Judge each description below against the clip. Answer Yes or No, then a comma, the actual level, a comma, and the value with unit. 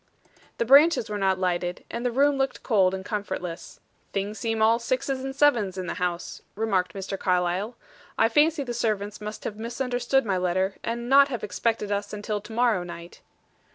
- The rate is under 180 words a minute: No, average, 185 wpm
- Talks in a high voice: Yes, high, 215 Hz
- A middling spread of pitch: Yes, average, 4.3 semitones